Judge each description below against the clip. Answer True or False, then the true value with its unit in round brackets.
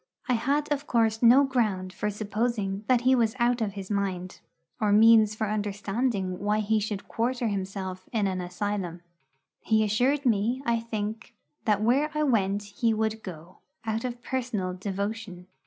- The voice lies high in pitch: True (215 Hz)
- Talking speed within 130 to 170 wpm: True (165 wpm)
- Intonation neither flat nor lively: True (3.0 semitones)